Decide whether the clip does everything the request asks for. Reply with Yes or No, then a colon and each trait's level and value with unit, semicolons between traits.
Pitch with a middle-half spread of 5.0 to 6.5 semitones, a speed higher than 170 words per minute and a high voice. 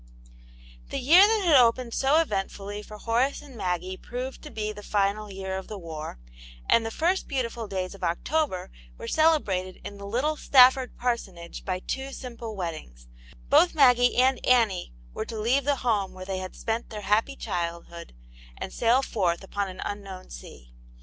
Yes: wide, 5.5 semitones; average, 180 wpm; high, 215 Hz